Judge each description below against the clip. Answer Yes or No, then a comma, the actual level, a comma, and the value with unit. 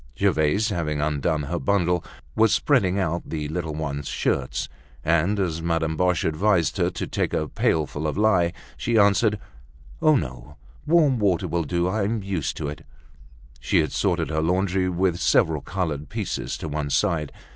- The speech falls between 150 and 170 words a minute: Yes, average, 165 wpm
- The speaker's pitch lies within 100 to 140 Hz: No, very low, 85 Hz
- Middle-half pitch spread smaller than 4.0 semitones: No, average, 4.3 semitones